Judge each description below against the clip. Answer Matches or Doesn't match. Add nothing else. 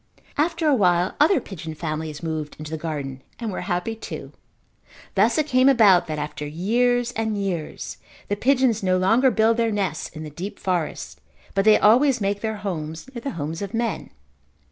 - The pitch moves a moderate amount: Doesn't match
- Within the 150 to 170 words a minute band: Doesn't match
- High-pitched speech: Matches